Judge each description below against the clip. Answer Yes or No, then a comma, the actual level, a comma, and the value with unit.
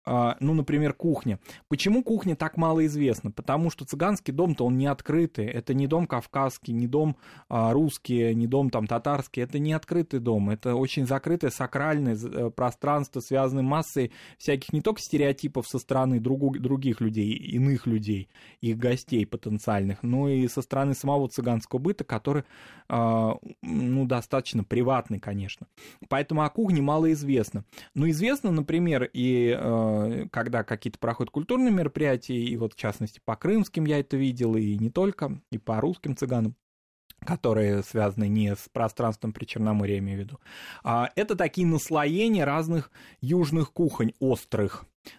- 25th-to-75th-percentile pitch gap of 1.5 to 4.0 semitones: No, average, 4.7 semitones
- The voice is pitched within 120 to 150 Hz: Yes, low, 130 Hz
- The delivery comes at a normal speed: Yes, average, 150 wpm